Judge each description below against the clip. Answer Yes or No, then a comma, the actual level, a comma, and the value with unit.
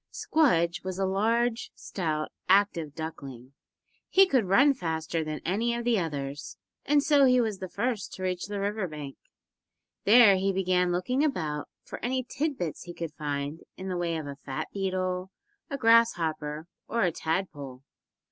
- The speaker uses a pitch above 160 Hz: Yes, medium, 185 Hz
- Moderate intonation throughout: No, wide, 6.4 semitones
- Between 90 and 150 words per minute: No, average, 170 wpm